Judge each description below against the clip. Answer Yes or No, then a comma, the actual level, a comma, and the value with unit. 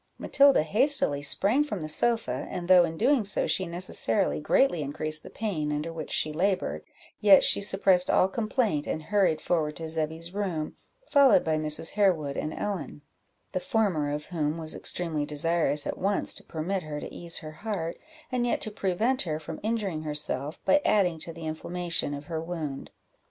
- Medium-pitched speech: Yes, medium, 170 Hz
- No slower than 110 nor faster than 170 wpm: No, average, 180 wpm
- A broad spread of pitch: No, average, 4.6 semitones